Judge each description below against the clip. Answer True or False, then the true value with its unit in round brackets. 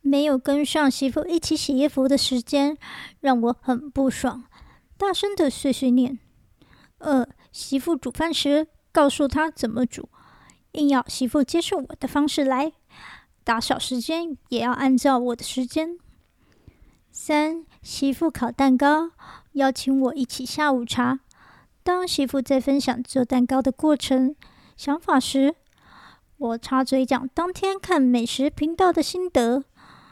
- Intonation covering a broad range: False (2.9 semitones)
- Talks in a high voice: True (275 Hz)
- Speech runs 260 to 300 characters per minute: False (205 characters per minute)